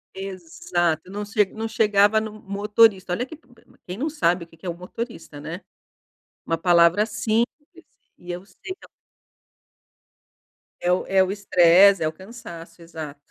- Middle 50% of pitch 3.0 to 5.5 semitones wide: Yes, average, 4.1 semitones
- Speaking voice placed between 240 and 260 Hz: No, high, 190 Hz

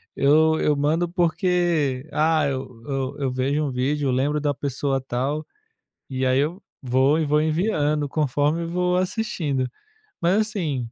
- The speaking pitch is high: No, medium, 150 Hz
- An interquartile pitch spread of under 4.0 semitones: Yes, average, 3.3 semitones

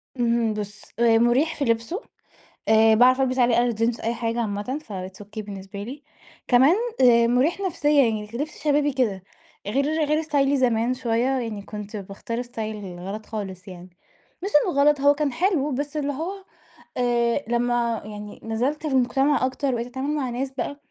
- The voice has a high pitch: Yes, high, 240 Hz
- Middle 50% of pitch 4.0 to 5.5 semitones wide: Yes, average, 4.3 semitones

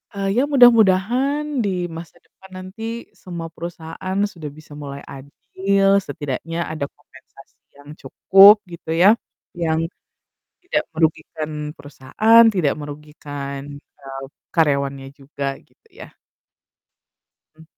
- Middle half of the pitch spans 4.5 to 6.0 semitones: Yes, average, 5.2 semitones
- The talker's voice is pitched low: No, medium, 160 Hz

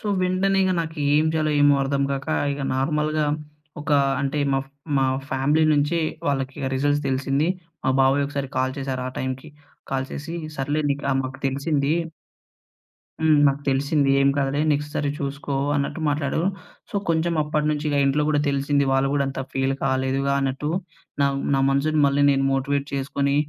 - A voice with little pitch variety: Yes, narrow, 1.7 semitones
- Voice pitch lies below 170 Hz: Yes, medium, 140 Hz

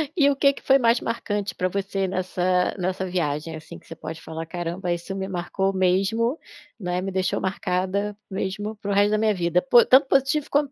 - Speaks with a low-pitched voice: No, high, 190 Hz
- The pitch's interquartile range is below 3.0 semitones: No, average, 3.3 semitones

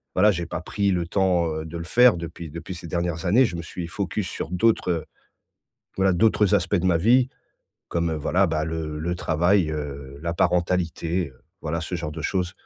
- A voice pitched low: Yes, very low, 85 Hz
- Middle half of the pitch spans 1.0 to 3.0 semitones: Yes, narrow, 2.4 semitones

